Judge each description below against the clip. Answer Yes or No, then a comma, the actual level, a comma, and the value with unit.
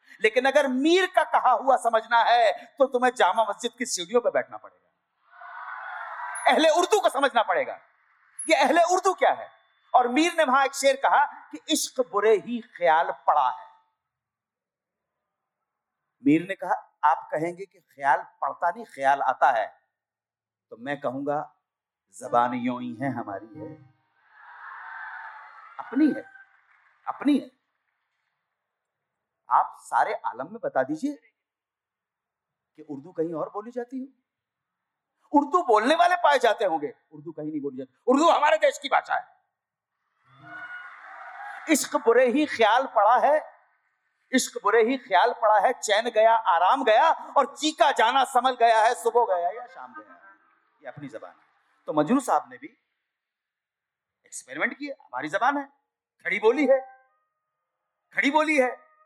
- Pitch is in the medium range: No, very high, 260 Hz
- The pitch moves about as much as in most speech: No, wide, 6.7 semitones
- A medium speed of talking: Yes, average, 145 wpm